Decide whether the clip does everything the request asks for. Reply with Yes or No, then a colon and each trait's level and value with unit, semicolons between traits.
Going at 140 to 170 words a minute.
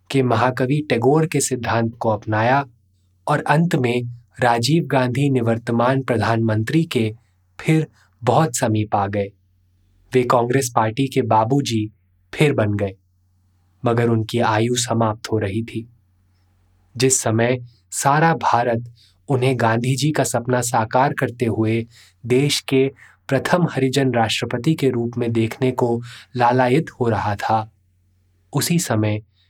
No: average, 130 wpm